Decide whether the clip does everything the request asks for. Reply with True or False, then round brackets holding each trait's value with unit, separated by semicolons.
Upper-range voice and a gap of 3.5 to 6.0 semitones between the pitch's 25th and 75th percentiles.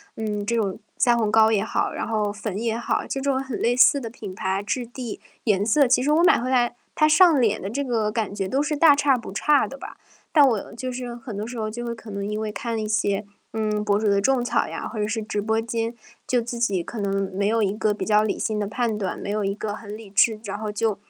False (220 Hz; 2.7 semitones)